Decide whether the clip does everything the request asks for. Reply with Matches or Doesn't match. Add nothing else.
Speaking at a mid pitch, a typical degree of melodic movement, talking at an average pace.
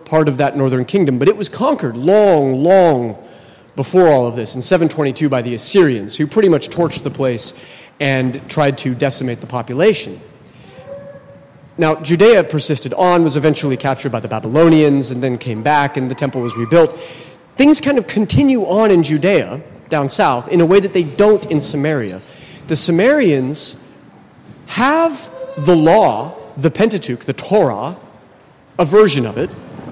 Matches